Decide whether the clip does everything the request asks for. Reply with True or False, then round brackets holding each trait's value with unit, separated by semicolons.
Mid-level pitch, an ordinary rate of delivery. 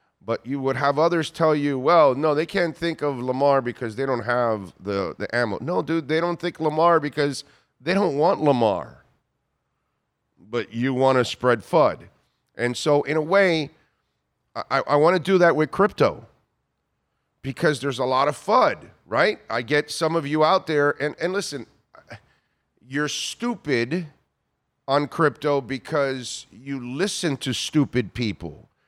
True (145 Hz; 160 wpm)